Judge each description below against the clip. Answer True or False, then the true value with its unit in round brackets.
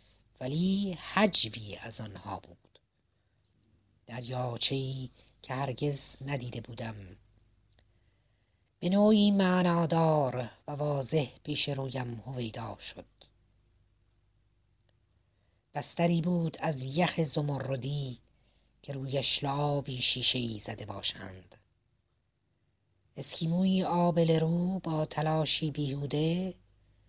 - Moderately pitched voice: False (125 Hz)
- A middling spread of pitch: False (6.0 semitones)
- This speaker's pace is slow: True (85 wpm)